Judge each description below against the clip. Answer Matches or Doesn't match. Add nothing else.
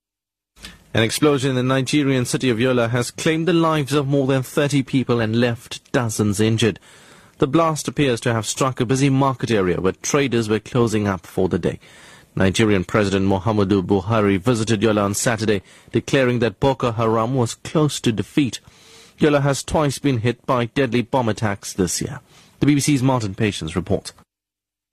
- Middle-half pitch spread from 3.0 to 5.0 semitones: Matches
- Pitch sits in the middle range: Doesn't match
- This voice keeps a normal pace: Matches